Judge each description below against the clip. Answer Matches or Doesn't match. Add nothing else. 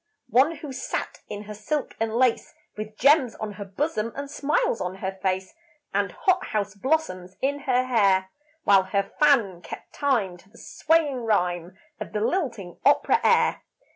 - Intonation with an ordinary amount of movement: Doesn't match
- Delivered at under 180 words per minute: Matches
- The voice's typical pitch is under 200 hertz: Doesn't match